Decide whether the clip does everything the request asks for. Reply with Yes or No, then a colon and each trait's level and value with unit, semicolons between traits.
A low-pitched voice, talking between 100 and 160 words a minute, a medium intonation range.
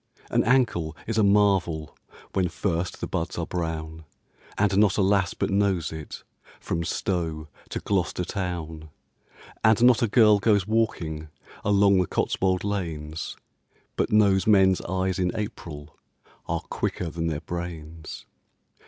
Yes: very low, 90 Hz; average, 140 wpm; average, 3.9 semitones